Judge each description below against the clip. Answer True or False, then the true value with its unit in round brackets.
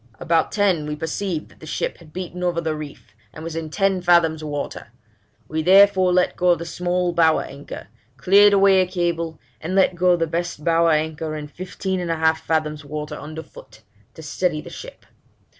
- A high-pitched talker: False (165 Hz)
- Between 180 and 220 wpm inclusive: True (190 wpm)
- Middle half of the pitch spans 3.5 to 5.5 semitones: False (2.6 semitones)